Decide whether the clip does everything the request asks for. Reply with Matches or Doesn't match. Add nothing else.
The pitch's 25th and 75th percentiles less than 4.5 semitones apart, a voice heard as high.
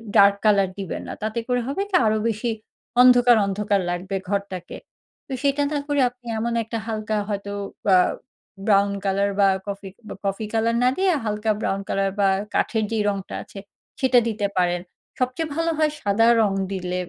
Matches